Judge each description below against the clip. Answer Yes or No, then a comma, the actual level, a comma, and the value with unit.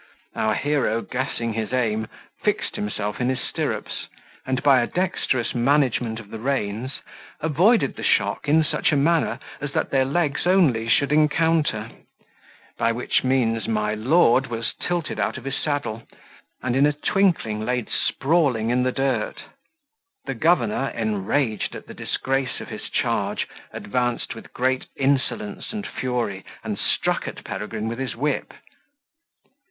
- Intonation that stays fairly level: No, average, 4.3 semitones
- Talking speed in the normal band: Yes, average, 150 wpm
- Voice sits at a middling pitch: No, low, 130 Hz